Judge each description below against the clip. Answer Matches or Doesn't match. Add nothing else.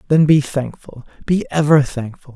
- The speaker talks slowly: Matches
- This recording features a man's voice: Matches